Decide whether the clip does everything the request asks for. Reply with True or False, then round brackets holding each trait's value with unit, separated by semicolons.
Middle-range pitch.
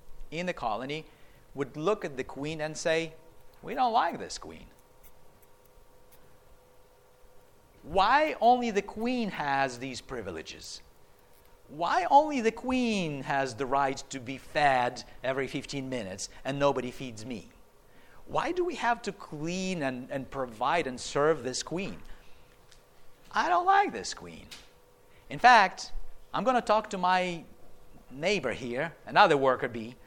True (150 Hz)